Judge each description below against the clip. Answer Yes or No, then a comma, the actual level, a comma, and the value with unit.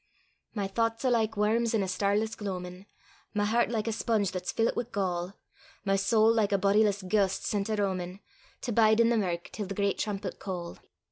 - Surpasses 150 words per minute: Yes, average, 200 wpm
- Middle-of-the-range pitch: No, high, 205 Hz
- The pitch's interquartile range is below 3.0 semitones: Yes, narrow, 2.4 semitones